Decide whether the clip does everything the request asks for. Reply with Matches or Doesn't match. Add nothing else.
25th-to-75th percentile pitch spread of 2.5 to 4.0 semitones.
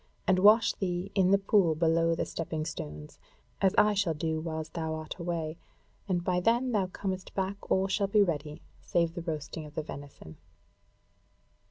Matches